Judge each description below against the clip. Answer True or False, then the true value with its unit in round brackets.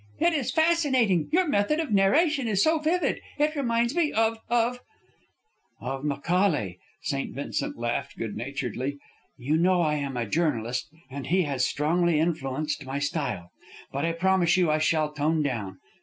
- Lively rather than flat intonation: True (8.9 semitones)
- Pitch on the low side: False (165 Hz)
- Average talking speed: True (165 wpm)